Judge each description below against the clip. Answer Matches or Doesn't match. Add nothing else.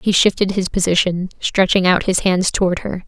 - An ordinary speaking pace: Matches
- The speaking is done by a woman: Matches